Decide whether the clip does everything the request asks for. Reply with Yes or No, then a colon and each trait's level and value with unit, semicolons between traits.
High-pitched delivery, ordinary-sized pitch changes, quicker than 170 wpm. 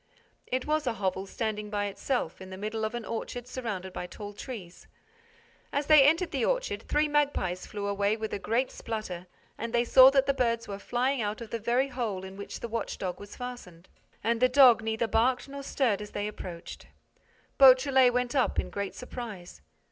Yes: high, 230 Hz; average, 4.1 semitones; average, 200 wpm